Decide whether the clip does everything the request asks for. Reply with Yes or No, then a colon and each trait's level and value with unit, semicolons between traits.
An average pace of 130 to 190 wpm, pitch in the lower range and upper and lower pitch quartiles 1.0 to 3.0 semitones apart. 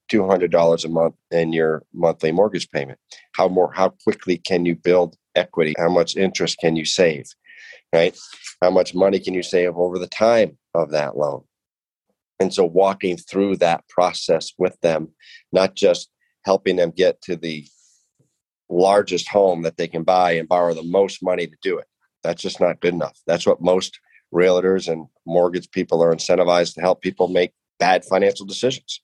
Yes: average, 175 wpm; very low, 90 Hz; narrow, 2.5 semitones